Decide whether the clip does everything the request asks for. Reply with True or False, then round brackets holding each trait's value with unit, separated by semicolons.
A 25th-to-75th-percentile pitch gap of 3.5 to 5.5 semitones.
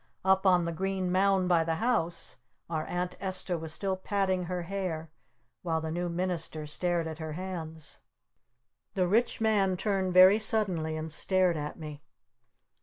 False (2.8 semitones)